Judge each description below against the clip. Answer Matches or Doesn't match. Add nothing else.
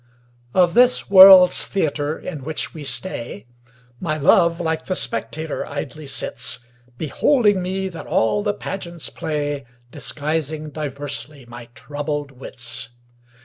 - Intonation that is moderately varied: Matches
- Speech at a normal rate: Doesn't match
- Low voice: Doesn't match